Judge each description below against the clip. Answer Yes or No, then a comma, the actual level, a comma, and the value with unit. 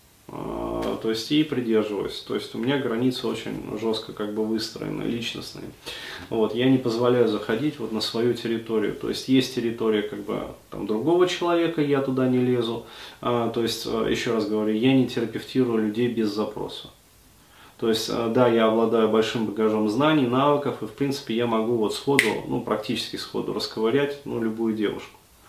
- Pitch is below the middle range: Yes, low, 115 Hz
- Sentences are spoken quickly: Yes, fast, 165 wpm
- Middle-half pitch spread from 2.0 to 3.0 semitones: Yes, narrow, 2.5 semitones